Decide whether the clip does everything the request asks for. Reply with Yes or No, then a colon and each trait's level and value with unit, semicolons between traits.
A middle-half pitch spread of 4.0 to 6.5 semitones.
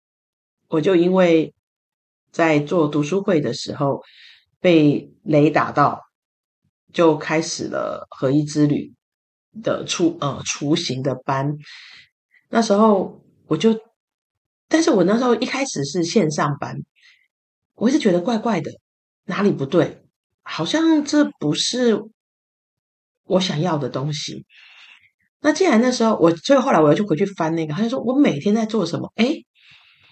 No: wide, 7.5 semitones